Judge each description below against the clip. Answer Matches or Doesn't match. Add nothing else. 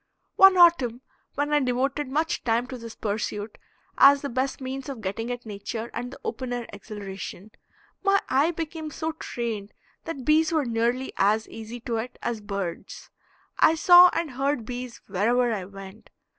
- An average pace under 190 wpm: Matches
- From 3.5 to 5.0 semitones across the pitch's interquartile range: Matches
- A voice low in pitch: Doesn't match